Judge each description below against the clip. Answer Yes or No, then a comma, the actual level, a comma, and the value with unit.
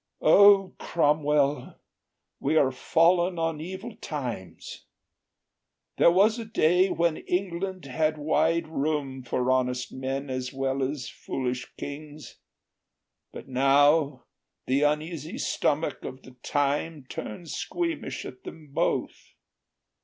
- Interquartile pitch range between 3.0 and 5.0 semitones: Yes, average, 3.9 semitones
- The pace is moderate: No, slow, 115 wpm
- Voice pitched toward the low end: No, medium, 150 Hz